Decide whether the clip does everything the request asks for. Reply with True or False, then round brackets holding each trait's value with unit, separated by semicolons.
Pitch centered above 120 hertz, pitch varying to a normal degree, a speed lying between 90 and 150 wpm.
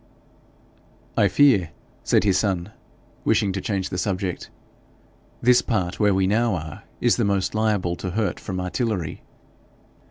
False (100 Hz; 3.1 semitones; 145 wpm)